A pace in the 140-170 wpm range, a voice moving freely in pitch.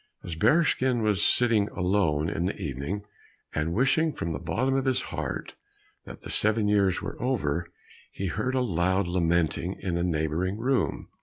Yes: average, 165 wpm; wide, 5.7 semitones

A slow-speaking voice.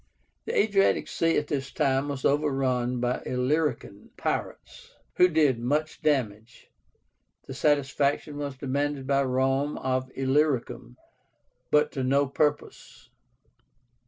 Yes: slow, 110 wpm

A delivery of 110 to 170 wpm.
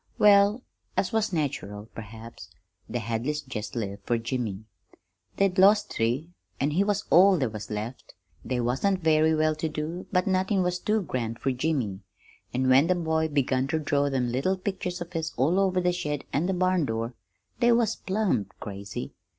No: average, 180 wpm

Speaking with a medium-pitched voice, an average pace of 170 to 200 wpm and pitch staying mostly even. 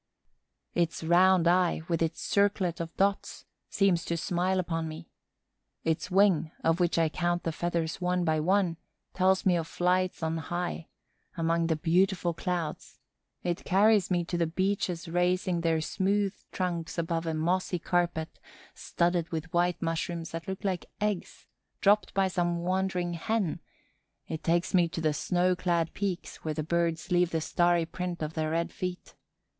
No: medium, 175 Hz; average, 160 wpm; narrow, 1.9 semitones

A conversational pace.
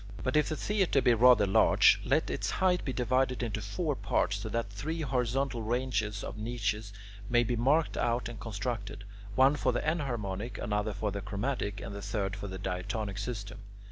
Yes: average, 185 wpm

